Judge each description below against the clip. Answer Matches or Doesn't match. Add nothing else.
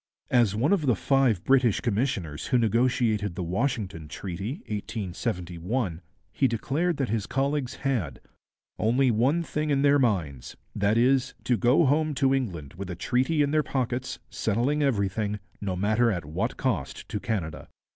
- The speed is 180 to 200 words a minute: Doesn't match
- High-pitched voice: Doesn't match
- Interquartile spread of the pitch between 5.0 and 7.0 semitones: Matches